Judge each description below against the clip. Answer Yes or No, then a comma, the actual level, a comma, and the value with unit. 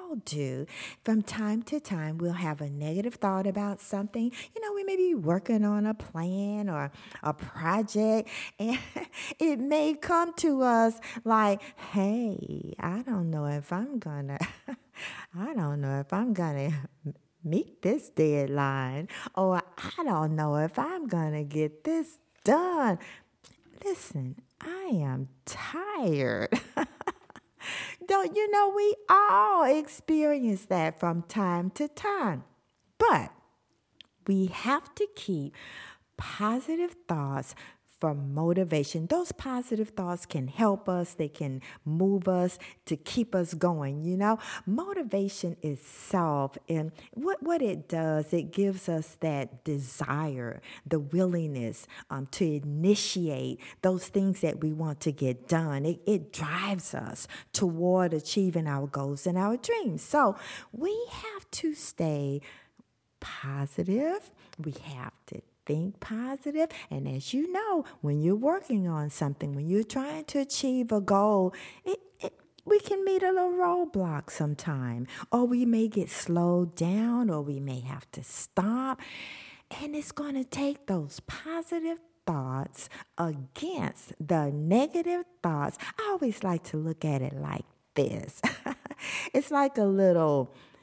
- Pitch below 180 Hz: No, high, 190 Hz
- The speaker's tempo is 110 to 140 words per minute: Yes, slow, 135 wpm